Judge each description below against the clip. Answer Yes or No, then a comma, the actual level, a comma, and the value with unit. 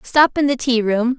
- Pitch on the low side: No, very high, 250 Hz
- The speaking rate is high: Yes, fast, 255 wpm